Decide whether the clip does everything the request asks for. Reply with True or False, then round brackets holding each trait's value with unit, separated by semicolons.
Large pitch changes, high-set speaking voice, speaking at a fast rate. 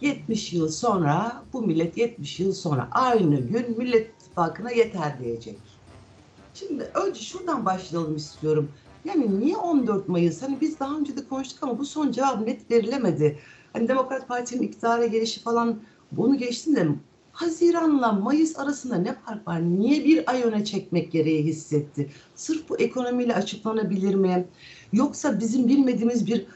True (7.5 semitones; 230 Hz; 150 wpm)